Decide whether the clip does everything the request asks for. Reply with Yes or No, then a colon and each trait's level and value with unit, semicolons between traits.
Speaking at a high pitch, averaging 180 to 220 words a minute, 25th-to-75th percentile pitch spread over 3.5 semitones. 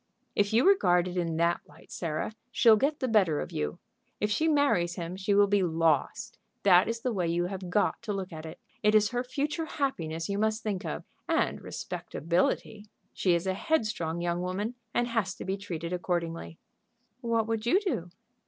Yes: high, 195 Hz; average, 195 wpm; average, 4.7 semitones